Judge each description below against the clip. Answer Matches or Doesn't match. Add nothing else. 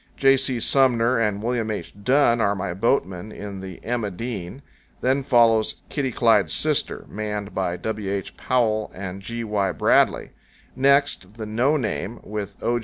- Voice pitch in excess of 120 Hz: Doesn't match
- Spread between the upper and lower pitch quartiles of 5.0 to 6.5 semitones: Doesn't match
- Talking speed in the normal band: Matches